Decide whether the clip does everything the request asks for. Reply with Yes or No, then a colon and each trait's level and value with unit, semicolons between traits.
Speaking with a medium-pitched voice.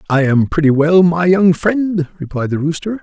Yes: medium, 165 Hz